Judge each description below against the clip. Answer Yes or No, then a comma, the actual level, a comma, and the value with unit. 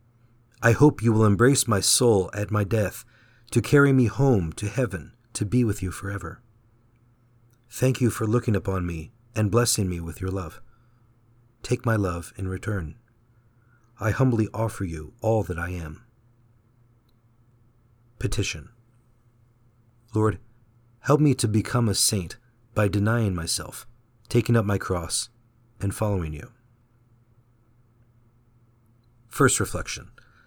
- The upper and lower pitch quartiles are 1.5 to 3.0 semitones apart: Yes, narrow, 2.5 semitones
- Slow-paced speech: Yes, slow, 130 wpm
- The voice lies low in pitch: Yes, low, 115 Hz